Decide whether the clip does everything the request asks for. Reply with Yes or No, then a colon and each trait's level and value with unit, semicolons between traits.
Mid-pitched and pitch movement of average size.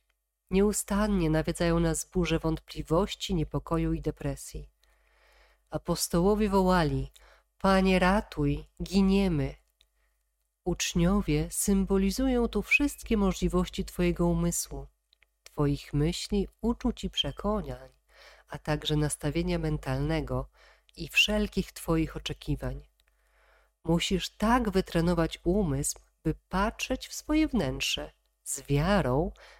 Yes: medium, 170 Hz; average, 4.5 semitones